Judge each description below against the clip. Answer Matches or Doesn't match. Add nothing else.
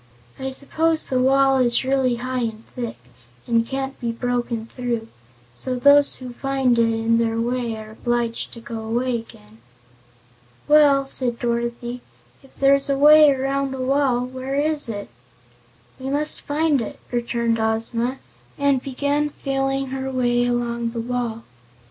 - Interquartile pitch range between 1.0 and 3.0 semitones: Matches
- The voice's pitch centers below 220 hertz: Doesn't match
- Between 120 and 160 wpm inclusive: Matches